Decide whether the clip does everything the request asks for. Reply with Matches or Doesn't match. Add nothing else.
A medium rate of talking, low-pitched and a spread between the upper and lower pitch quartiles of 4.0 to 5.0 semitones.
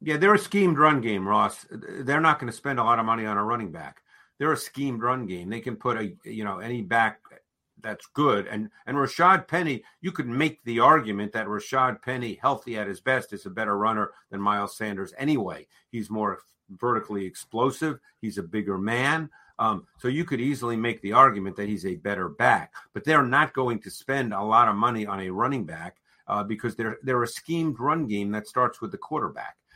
Doesn't match